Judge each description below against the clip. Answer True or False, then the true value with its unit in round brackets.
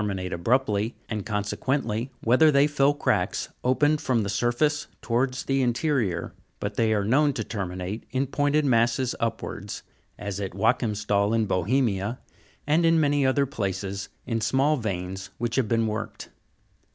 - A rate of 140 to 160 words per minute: True (150 wpm)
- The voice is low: True (115 Hz)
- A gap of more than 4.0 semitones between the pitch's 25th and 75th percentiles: True (4.9 semitones)